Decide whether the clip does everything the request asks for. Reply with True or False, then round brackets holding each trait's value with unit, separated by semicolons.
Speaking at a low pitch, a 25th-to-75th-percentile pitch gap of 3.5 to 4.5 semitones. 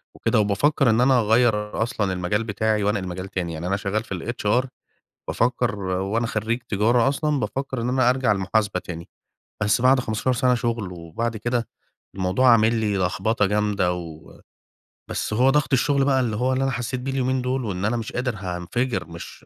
True (110 Hz; 4.1 semitones)